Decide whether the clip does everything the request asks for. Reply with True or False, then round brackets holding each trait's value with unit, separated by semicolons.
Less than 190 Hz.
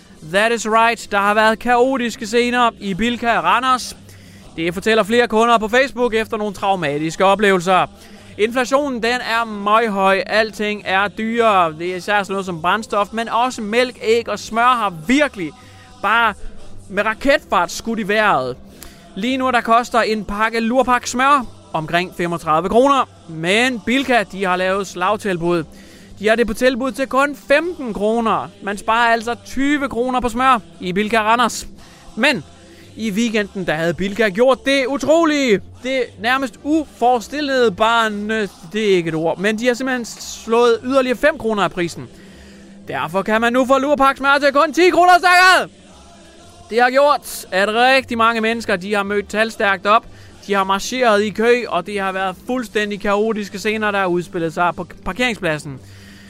False (220 Hz)